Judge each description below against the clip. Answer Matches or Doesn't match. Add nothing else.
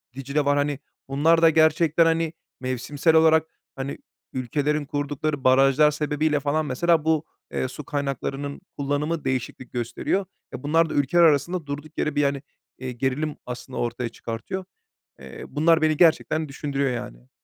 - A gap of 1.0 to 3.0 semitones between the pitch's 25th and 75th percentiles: Matches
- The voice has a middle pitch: Matches